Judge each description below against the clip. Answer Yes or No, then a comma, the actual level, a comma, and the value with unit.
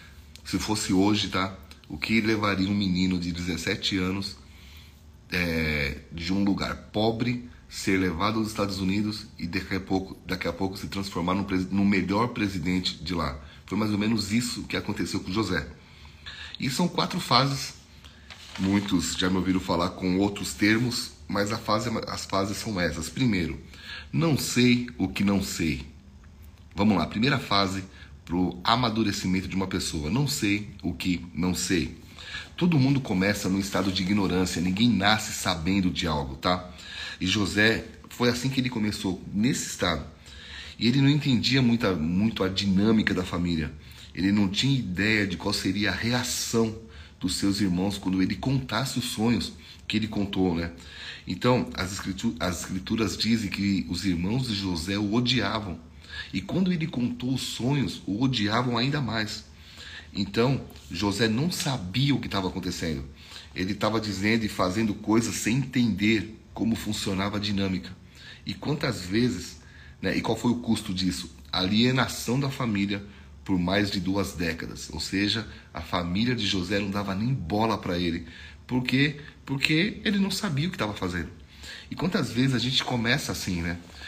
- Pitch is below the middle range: Yes, low, 100 Hz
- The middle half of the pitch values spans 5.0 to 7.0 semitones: No, average, 4.3 semitones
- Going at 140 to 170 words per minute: Yes, average, 165 wpm